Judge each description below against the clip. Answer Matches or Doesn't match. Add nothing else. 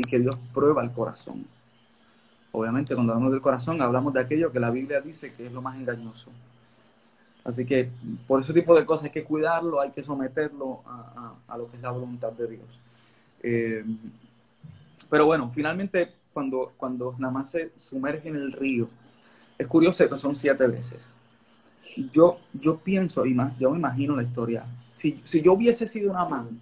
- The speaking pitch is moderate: Doesn't match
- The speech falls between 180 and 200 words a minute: Matches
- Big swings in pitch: Doesn't match